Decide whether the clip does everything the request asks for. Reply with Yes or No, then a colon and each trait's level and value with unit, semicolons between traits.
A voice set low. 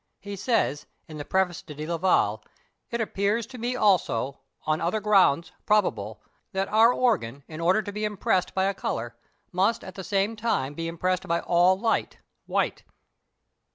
No: high, 190 Hz